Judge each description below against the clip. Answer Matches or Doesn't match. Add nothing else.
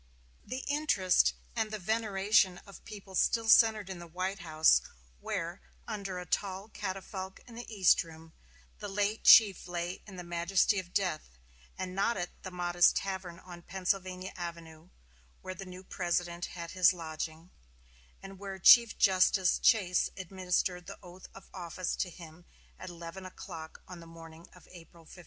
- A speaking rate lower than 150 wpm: Doesn't match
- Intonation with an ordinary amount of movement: Doesn't match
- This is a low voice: Doesn't match